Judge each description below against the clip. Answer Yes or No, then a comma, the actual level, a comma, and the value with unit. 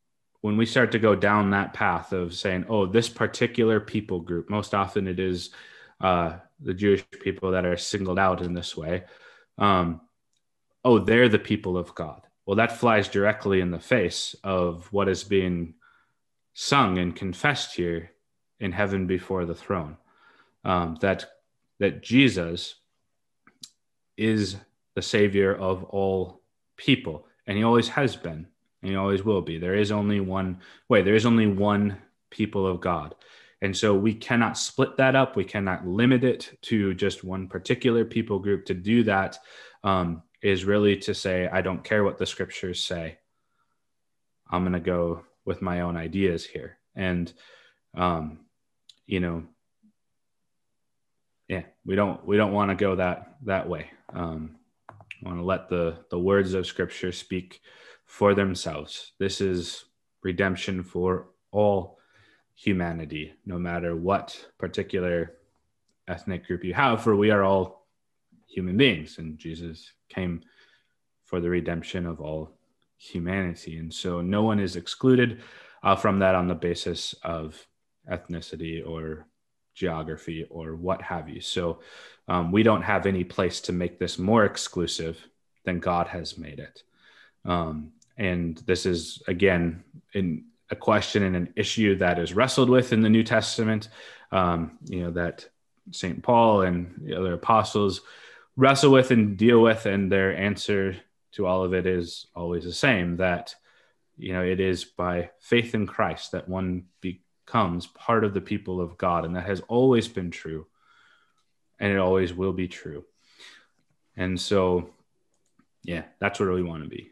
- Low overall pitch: Yes, very low, 95 Hz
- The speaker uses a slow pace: No, average, 155 wpm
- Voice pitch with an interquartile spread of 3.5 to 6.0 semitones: No, average, 2.9 semitones